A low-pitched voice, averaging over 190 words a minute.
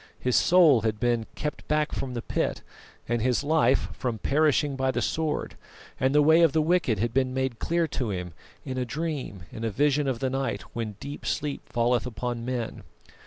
Yes: low, 130 Hz; average, 200 wpm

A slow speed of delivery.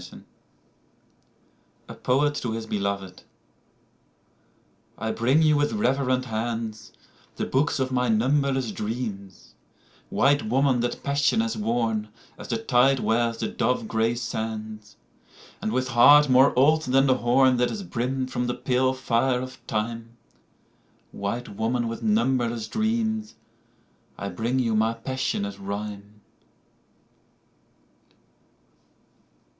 Yes: slow, 120 wpm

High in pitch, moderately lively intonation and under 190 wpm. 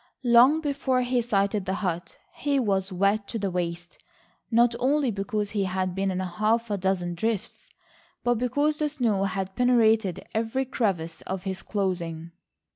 Yes: high, 205 Hz; average, 4.4 semitones; average, 160 wpm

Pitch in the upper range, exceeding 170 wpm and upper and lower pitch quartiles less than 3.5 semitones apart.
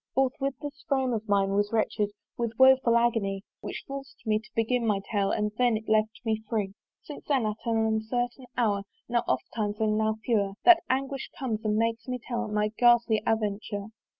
Yes: high, 225 Hz; average, 190 wpm; average, 2.7 semitones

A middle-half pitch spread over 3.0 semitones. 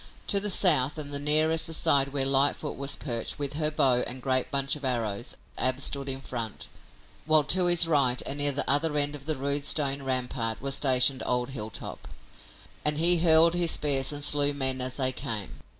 No: narrow, 2.6 semitones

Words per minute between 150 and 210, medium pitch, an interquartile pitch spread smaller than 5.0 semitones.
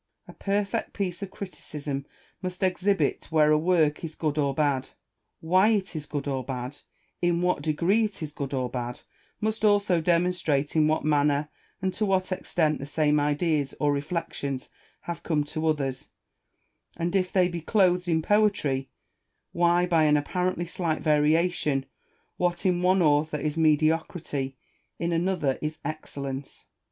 Yes: average, 155 wpm; medium, 160 Hz; average, 3.6 semitones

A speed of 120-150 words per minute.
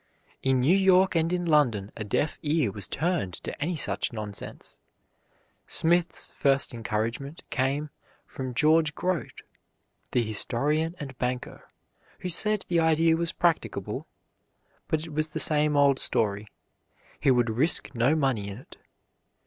Yes: average, 140 wpm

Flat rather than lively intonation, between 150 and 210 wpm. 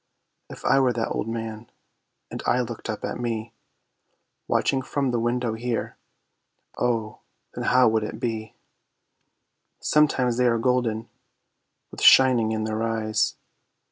No: narrow, 2.1 semitones; average, 140 wpm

